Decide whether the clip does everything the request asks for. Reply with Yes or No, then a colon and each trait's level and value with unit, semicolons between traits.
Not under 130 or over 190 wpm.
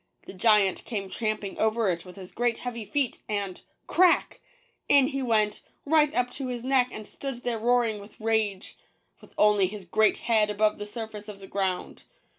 No: fast, 205 wpm